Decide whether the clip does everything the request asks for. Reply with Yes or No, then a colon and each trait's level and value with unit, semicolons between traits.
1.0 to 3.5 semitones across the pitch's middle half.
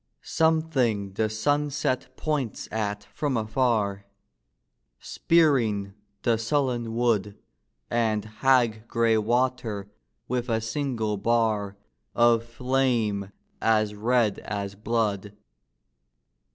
Yes: average, 3.2 semitones